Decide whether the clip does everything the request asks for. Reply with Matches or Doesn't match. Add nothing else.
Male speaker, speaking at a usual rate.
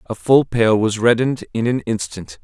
Matches